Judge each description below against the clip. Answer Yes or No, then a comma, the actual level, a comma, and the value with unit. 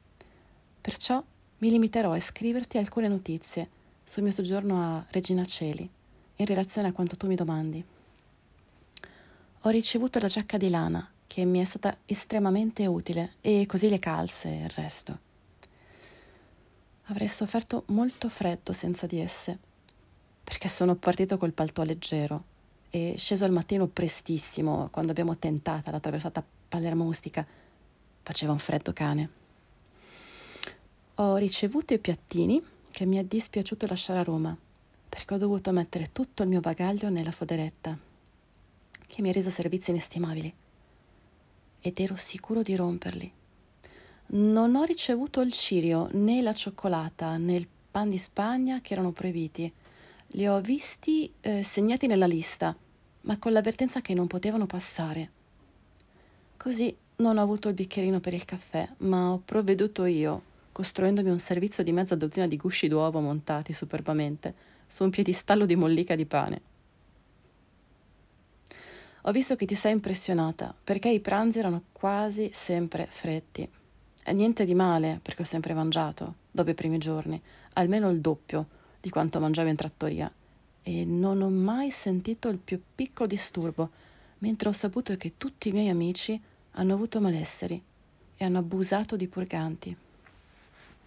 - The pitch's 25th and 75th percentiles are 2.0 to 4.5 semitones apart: Yes, average, 4.0 semitones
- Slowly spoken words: No, average, 145 wpm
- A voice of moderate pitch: Yes, medium, 180 Hz